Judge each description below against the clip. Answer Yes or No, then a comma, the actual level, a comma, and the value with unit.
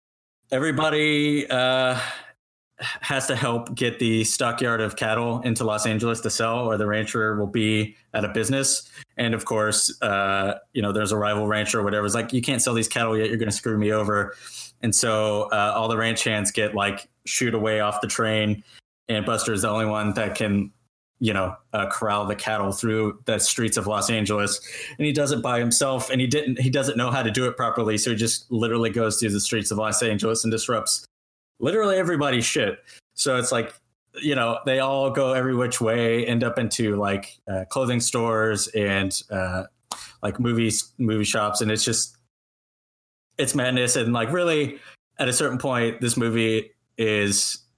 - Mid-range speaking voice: No, low, 115 Hz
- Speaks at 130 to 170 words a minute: No, average, 195 wpm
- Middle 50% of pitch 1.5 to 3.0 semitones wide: Yes, narrow, 2.6 semitones